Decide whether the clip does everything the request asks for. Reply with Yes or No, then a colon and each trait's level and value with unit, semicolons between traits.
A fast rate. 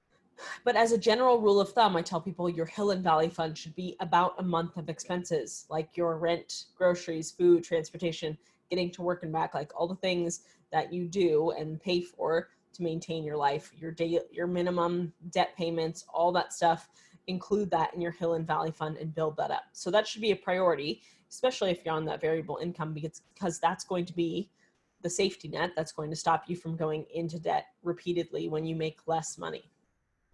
Yes: fast, 210 wpm